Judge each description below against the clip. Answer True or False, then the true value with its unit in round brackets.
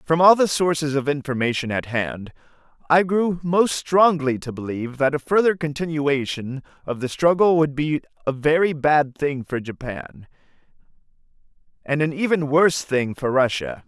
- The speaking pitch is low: False (150 Hz)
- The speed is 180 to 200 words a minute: False (155 wpm)